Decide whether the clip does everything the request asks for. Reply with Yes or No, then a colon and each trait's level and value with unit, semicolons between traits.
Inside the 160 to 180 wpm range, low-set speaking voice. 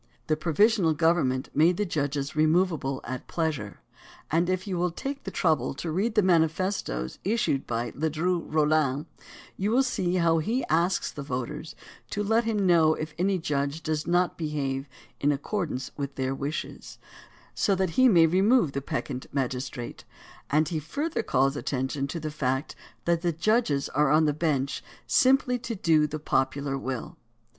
No: average, 165 wpm; medium, 155 Hz